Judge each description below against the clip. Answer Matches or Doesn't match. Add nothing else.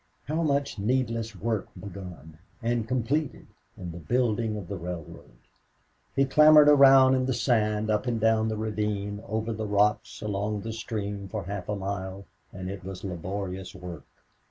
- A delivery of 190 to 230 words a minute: Doesn't match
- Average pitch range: Matches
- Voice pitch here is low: Matches